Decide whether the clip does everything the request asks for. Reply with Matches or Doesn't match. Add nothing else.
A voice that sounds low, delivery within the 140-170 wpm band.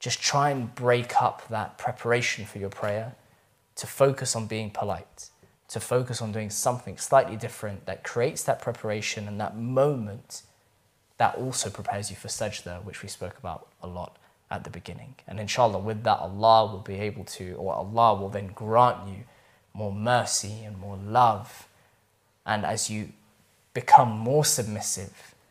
Matches